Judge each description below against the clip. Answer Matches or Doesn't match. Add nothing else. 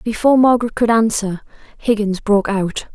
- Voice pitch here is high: Matches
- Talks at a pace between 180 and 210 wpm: Doesn't match